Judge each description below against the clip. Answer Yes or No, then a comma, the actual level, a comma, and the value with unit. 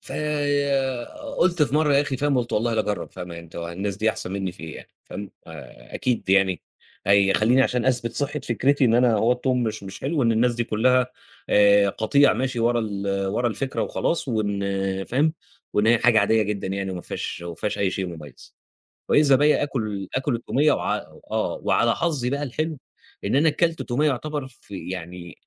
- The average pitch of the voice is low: Yes, low, 120 Hz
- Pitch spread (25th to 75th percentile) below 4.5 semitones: No, wide, 5.6 semitones